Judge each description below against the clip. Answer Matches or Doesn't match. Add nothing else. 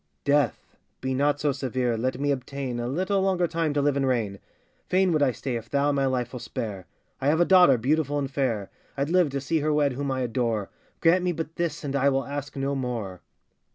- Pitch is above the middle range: Doesn't match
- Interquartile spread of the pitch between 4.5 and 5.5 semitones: Doesn't match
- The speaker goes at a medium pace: Doesn't match